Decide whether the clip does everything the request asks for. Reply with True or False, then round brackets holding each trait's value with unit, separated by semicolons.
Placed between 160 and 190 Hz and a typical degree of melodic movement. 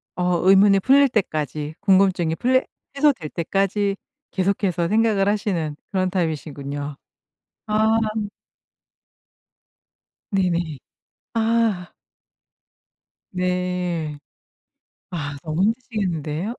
True (185 Hz; 4.3 semitones)